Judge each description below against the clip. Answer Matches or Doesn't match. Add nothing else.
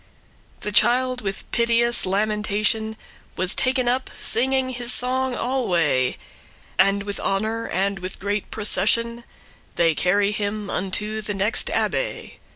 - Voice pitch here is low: Doesn't match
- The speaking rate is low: Matches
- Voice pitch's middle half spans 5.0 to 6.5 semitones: Doesn't match